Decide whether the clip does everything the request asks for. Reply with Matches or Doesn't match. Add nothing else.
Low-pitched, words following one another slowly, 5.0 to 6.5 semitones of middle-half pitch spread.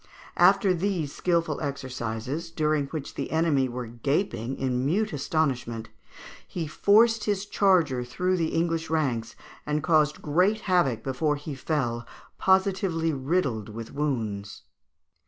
Doesn't match